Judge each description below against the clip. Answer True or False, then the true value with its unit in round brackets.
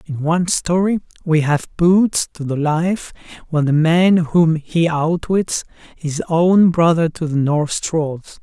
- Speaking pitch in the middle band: True (165 Hz)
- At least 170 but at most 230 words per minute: False (155 wpm)